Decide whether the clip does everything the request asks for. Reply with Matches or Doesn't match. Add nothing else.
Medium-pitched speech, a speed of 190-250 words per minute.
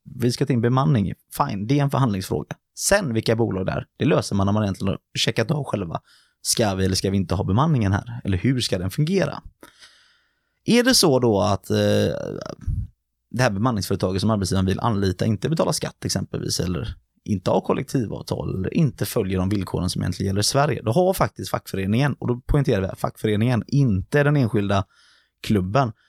Doesn't match